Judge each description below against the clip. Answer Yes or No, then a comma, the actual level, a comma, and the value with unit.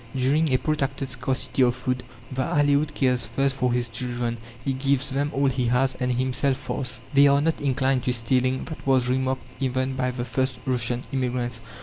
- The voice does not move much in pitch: Yes, narrow, 1.5 semitones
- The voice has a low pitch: Yes, low, 130 Hz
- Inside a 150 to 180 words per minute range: No, average, 190 wpm